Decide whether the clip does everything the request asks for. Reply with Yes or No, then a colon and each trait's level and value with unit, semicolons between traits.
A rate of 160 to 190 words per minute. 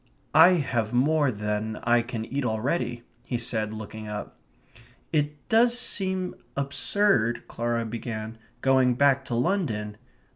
No: slow, 135 wpm